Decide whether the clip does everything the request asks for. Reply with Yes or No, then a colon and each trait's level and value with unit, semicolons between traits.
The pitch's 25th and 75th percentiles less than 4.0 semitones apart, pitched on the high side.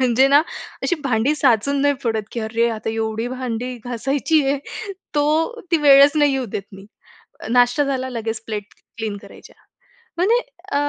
No: average, 4.3 semitones; very high, 255 Hz